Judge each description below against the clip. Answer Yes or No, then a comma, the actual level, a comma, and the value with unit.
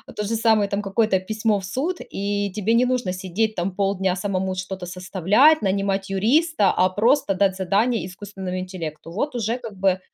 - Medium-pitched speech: No, high, 200 Hz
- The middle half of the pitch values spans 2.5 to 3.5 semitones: Yes, average, 3.0 semitones